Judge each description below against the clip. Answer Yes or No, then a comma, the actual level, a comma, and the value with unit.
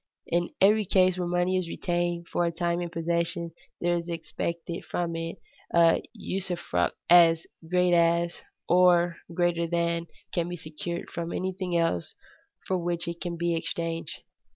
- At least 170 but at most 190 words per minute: No, average, 155 wpm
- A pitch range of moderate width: No, narrow, 0.9 semitones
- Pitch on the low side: No, medium, 170 Hz